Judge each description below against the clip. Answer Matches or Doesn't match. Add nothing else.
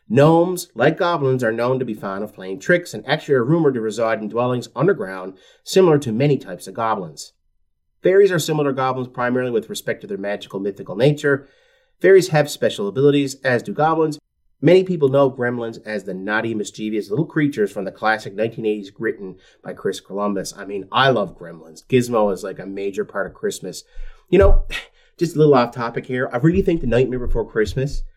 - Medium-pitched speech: Doesn't match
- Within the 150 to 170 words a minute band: Doesn't match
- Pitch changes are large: Matches